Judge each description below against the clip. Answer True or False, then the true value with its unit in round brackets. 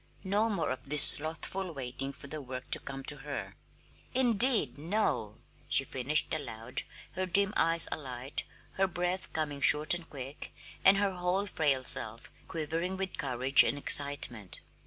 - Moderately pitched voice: True (150 Hz)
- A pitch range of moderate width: False (5.7 semitones)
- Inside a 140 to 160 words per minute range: True (155 wpm)